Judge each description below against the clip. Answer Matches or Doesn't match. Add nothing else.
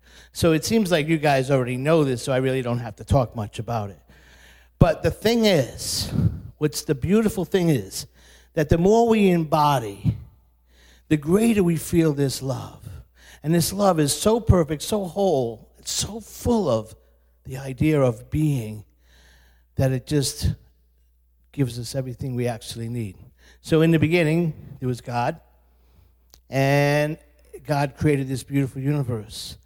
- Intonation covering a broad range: Matches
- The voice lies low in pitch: Matches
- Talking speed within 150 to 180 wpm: Matches